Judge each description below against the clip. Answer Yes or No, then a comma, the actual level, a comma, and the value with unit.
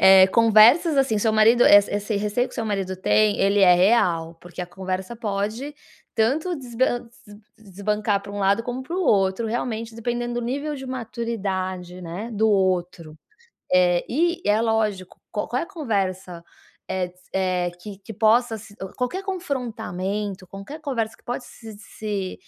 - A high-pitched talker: Yes, high, 215 Hz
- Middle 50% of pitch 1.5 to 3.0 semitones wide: No, average, 3.9 semitones